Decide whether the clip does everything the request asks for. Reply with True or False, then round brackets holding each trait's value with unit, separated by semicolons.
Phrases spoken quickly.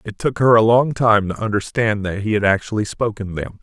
True (230 wpm)